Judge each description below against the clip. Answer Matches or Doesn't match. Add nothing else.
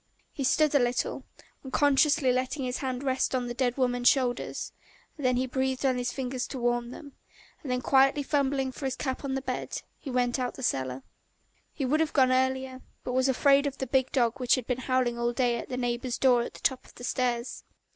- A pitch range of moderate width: Doesn't match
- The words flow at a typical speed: Doesn't match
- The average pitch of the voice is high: Matches